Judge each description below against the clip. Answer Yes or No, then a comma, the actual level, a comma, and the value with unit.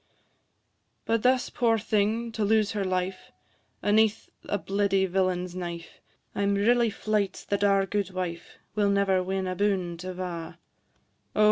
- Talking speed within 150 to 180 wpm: No, average, 140 wpm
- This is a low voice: No, high, 200 Hz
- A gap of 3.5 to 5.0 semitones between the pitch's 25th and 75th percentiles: No, narrow, 2.4 semitones